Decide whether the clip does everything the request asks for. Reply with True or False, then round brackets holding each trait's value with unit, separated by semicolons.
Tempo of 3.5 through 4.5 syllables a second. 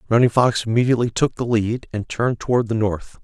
False (6.1 syllables/s)